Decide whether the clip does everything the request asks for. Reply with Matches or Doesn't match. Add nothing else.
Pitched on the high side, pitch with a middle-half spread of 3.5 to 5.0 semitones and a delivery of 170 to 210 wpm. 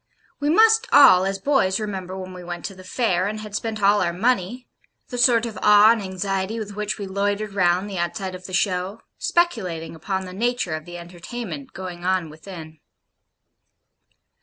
Doesn't match